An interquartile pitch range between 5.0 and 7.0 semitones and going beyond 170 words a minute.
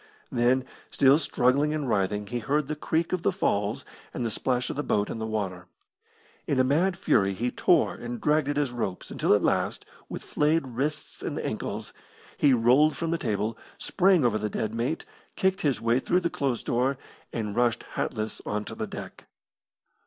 Yes: average, 5.3 semitones; average, 190 wpm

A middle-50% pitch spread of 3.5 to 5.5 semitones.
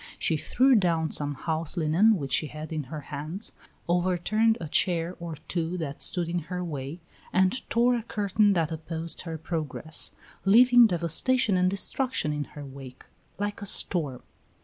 Yes: average, 4.4 semitones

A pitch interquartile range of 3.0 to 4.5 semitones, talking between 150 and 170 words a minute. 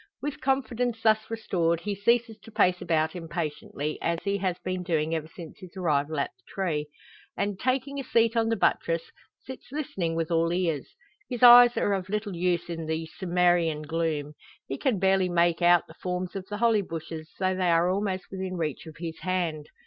No: average, 4.1 semitones; average, 195 wpm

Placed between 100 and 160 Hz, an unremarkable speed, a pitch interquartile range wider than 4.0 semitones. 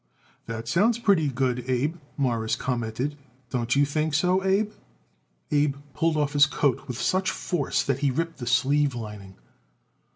Yes: medium, 140 Hz; average, 155 wpm; average, 4.6 semitones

